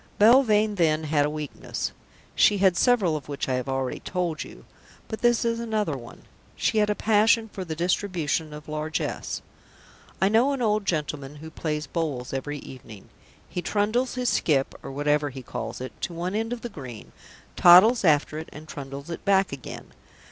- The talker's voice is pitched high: No, medium, 165 Hz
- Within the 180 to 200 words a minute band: Yes, average, 185 wpm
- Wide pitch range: Yes, wide, 6.2 semitones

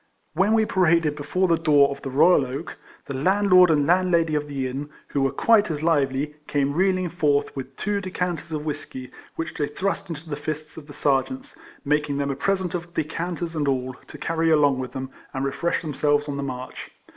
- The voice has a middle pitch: Yes, medium, 150 Hz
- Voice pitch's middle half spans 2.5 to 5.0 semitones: Yes, average, 3.8 semitones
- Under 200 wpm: No, fast, 205 wpm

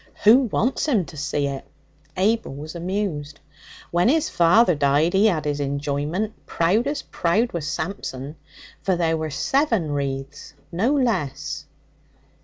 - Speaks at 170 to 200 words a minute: No, average, 140 wpm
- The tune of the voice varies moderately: No, wide, 6.6 semitones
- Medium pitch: Yes, medium, 170 Hz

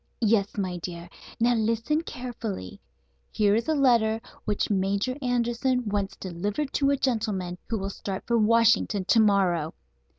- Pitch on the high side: Yes, high, 220 Hz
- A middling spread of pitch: Yes, average, 3.5 semitones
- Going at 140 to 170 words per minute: Yes, average, 145 wpm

